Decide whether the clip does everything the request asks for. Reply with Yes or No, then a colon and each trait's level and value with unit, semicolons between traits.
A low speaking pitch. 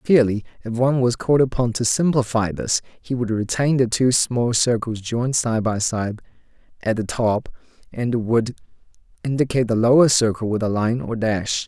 Yes: low, 115 Hz